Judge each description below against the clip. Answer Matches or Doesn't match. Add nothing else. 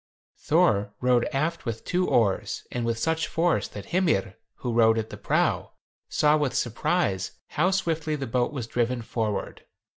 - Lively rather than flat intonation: Matches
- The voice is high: Doesn't match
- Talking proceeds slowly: Doesn't match